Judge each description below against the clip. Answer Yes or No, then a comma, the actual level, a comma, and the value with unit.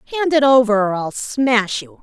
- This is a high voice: Yes, high, 230 Hz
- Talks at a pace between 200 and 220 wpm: Yes, fast, 205 wpm